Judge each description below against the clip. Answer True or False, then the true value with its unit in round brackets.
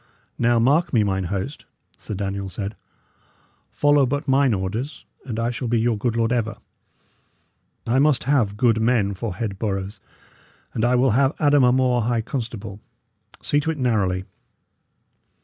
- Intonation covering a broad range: False (4.1 semitones)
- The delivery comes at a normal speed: True (160 wpm)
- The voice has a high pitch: False (115 Hz)